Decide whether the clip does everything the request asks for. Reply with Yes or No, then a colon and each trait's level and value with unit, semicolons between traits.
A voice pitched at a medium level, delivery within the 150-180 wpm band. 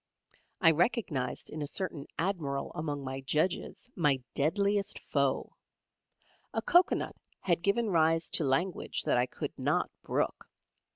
No: medium, 160 Hz; slow, 135 wpm